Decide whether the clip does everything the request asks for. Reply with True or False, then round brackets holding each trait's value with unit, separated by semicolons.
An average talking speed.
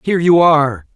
True (190 wpm)